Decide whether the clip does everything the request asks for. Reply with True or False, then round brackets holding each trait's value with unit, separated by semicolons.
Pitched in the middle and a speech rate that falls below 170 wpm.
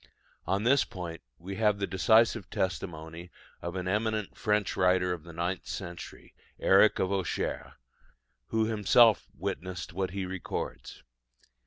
False (95 Hz; 135 wpm)